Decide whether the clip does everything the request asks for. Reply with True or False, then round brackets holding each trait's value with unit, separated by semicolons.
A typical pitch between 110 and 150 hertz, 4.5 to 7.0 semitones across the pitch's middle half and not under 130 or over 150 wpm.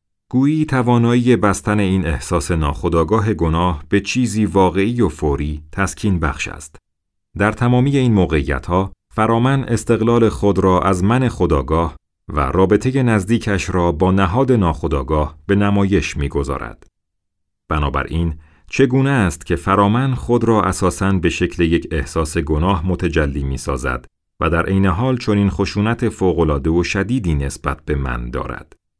False (95 Hz; 5.0 semitones; 140 wpm)